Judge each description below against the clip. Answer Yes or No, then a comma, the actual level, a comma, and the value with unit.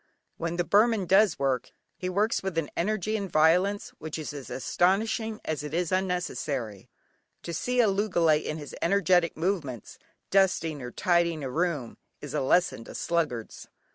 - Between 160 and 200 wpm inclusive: Yes, average, 165 wpm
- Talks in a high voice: No, medium, 170 Hz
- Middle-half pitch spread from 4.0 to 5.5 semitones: Yes, average, 4.3 semitones